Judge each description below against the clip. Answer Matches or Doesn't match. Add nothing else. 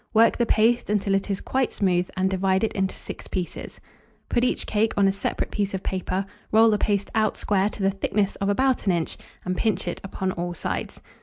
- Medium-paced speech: Doesn't match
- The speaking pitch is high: Matches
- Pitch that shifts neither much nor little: Doesn't match